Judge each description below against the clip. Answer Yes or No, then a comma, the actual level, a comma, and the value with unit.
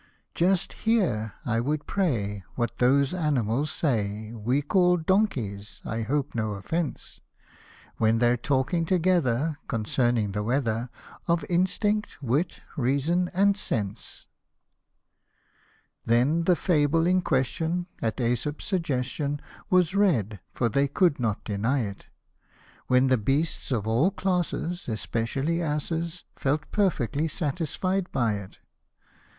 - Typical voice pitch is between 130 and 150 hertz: Yes, medium, 140 Hz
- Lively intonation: Yes, wide, 6.8 semitones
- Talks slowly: Yes, slow, 125 wpm